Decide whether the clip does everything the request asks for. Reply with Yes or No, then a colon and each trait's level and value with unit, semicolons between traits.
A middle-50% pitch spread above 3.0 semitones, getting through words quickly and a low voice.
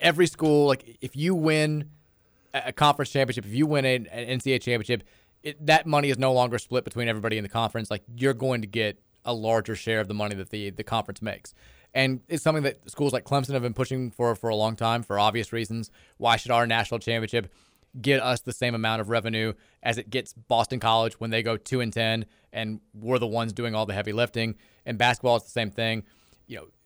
No: average, 2.7 semitones; fast, 225 wpm; low, 115 Hz